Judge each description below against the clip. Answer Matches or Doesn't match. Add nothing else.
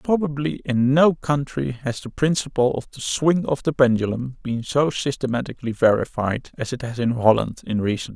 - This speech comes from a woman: Doesn't match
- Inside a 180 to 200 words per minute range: Matches